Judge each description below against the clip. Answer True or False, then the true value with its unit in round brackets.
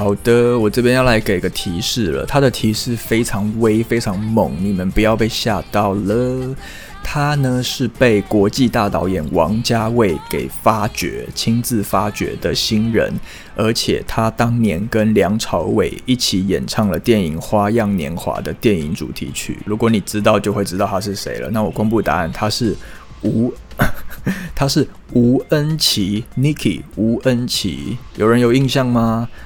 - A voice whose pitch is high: False (110 Hz)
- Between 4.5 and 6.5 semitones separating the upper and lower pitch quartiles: False (2.9 semitones)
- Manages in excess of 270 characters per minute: False (240 characters per minute)